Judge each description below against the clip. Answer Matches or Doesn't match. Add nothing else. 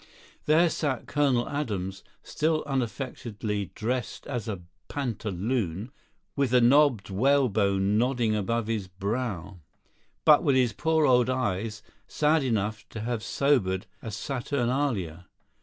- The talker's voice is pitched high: Doesn't match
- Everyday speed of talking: Doesn't match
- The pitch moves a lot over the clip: Doesn't match